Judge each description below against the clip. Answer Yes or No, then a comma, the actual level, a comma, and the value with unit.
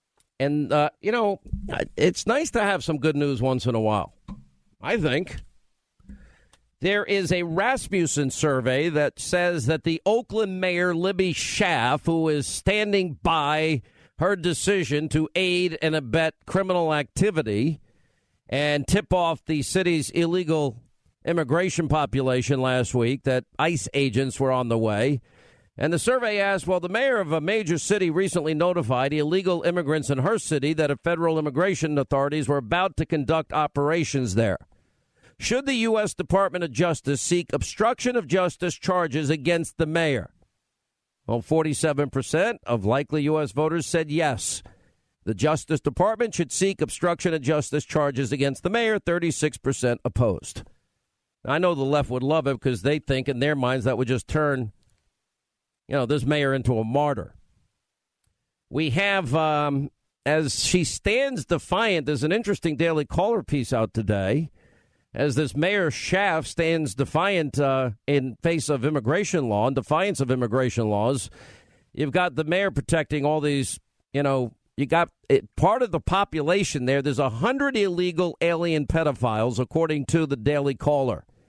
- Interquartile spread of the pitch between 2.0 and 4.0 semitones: No, average, 4.4 semitones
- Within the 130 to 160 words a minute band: Yes, average, 155 wpm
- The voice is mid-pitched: Yes, medium, 155 Hz